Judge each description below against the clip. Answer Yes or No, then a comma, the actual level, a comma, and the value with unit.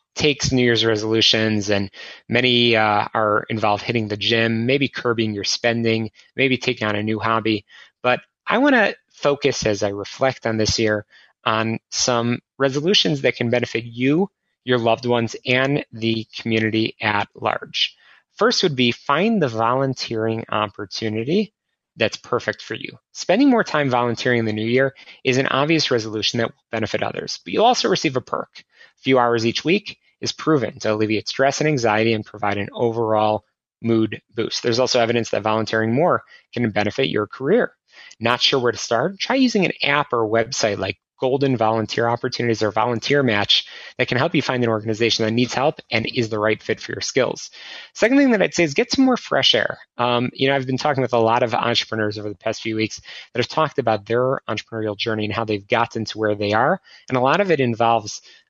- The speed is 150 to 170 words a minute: No, average, 200 wpm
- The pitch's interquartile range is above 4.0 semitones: No, average, 3.3 semitones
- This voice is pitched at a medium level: No, low, 115 Hz